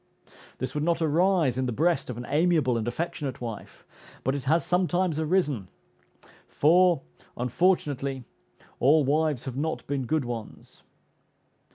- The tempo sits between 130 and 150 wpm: Yes, average, 140 wpm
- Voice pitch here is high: No, medium, 150 Hz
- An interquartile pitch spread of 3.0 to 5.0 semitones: Yes, average, 4.7 semitones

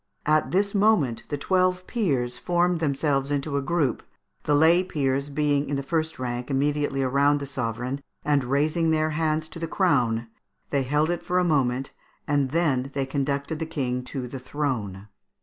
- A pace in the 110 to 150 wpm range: No, average, 175 wpm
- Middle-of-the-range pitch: Yes, medium, 145 Hz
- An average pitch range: Yes, average, 3.2 semitones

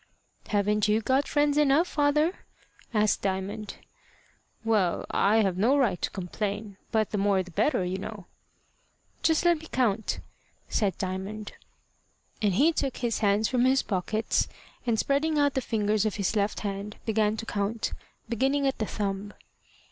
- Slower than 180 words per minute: Yes, average, 155 wpm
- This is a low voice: No, high, 215 Hz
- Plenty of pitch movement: No, average, 4.7 semitones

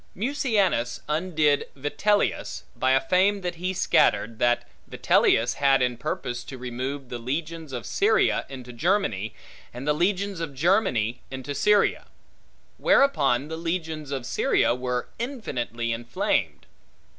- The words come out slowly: Yes, slow, 130 wpm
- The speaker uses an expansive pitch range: Yes, wide, 6.9 semitones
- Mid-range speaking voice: Yes, medium, 145 Hz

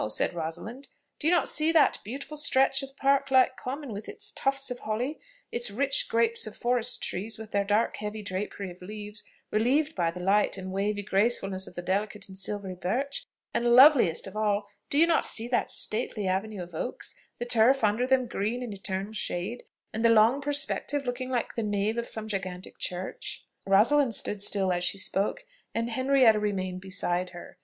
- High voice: Yes, high, 220 Hz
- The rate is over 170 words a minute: Yes, average, 190 wpm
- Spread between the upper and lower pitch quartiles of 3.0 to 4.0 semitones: No, average, 4.8 semitones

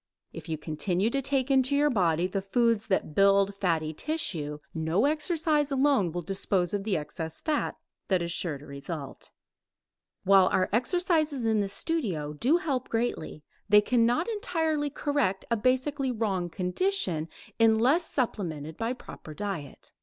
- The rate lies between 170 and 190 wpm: No, average, 150 wpm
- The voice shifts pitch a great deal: Yes, wide, 8.0 semitones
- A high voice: Yes, high, 210 Hz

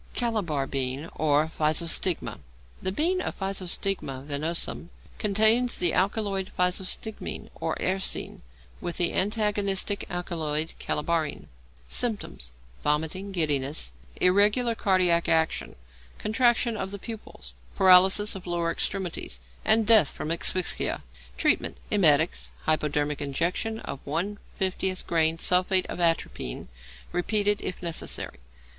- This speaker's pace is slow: Yes, slow, 105 wpm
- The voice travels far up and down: No, average, 4.4 semitones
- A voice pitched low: No, medium, 180 Hz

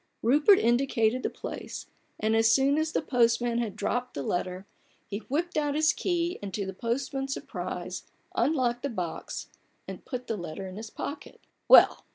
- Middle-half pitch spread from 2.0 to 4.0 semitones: No, average, 4.5 semitones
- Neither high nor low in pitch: No, high, 240 Hz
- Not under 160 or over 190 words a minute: Yes, average, 180 wpm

